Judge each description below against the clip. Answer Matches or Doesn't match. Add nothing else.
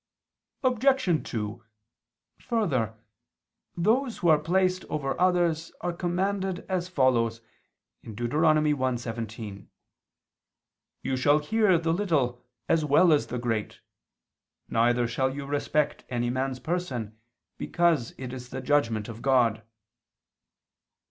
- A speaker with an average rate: Doesn't match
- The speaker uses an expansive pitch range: Matches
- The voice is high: Doesn't match